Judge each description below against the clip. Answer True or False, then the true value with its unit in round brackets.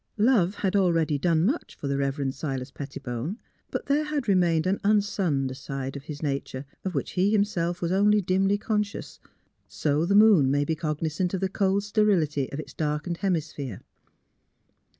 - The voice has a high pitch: False (170 Hz)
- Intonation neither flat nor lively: False (5.8 semitones)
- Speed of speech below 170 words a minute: False (180 wpm)